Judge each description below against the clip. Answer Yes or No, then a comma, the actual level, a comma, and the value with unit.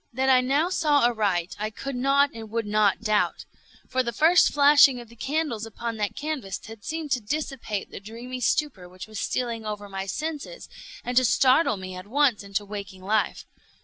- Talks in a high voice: Yes, high, 235 Hz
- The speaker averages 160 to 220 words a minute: Yes, average, 190 wpm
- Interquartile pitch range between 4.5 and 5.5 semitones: Yes, average, 5.2 semitones